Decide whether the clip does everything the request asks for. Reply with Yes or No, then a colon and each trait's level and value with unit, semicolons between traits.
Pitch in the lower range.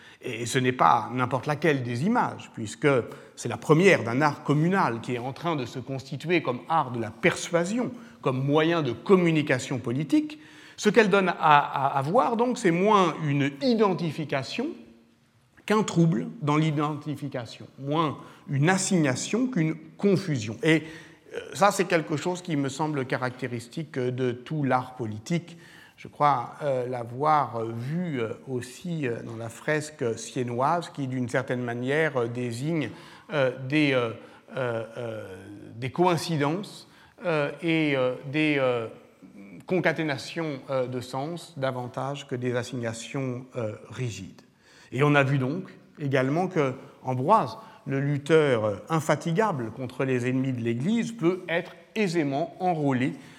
No: medium, 145 Hz